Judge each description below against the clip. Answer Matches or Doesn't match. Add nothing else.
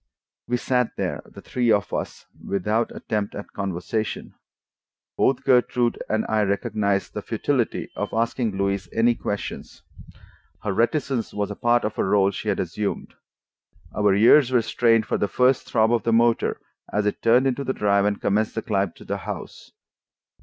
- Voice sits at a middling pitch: Doesn't match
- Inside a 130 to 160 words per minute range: Doesn't match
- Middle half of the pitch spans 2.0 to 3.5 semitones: Matches